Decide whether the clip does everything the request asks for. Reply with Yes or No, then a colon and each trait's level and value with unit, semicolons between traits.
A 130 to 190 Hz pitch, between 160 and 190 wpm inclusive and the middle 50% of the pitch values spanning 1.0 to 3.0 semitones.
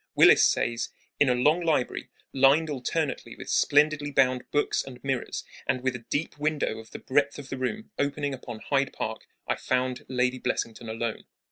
Yes: low, 135 Hz; average, 175 wpm; average, 2.7 semitones